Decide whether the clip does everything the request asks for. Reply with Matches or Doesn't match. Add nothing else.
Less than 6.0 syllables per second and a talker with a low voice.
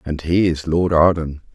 Matches